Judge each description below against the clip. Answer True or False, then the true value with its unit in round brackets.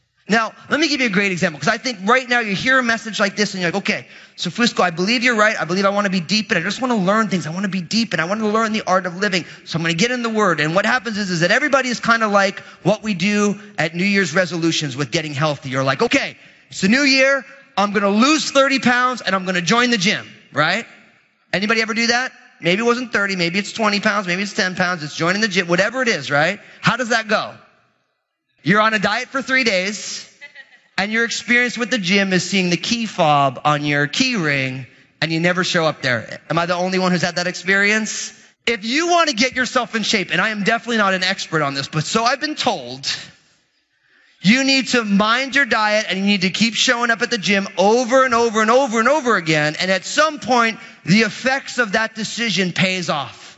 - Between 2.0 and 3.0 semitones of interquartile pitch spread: False (4.5 semitones)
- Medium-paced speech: False (255 wpm)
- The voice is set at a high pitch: True (205 Hz)